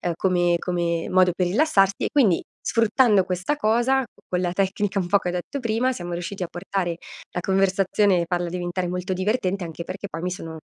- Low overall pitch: No, medium, 185 Hz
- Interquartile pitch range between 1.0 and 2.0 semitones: No, narrow, 2.6 semitones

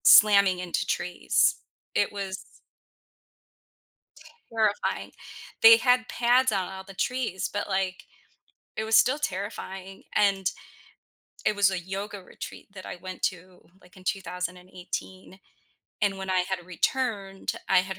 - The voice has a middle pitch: No, high, 195 Hz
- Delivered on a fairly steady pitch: Yes, narrow, 2.0 semitones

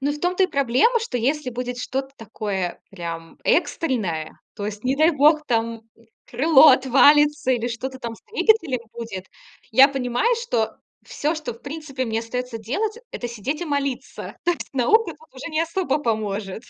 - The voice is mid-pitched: No, very high, 260 Hz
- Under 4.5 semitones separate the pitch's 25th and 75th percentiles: No, average, 5.0 semitones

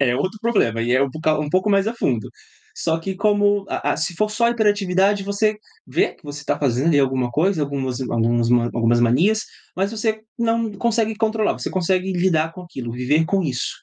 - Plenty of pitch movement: Yes, wide, 7.7 semitones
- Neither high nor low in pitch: Yes, medium, 175 Hz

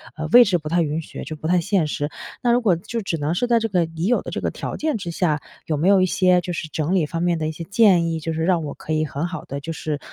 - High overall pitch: No, medium, 170 Hz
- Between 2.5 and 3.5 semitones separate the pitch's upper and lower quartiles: Yes, average, 3.1 semitones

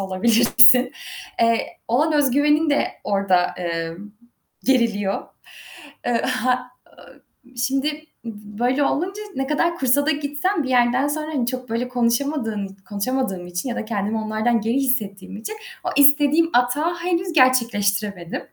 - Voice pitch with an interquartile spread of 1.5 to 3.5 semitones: No, average, 5.3 semitones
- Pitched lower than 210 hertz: No, very high, 250 Hz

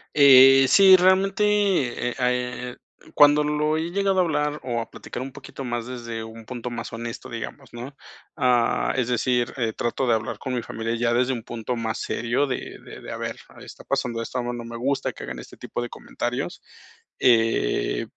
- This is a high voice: No, low, 125 Hz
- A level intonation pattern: No, average, 3.4 semitones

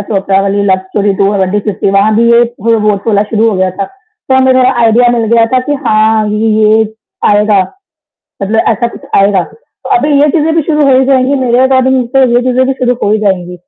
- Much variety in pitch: No, average, 4.2 semitones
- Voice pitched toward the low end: No, high, 220 Hz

